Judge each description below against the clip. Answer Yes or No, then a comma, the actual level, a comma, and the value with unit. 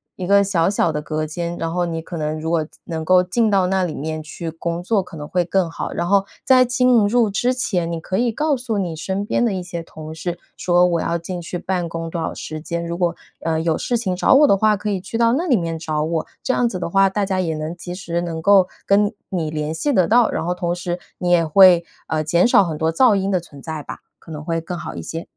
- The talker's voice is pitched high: No, medium, 175 Hz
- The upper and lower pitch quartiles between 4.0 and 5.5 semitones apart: No, average, 3.3 semitones